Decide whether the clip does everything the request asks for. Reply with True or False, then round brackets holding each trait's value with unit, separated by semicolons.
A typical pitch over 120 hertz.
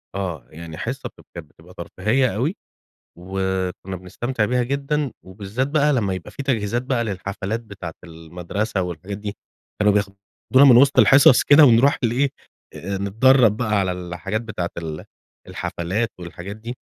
False (105 Hz)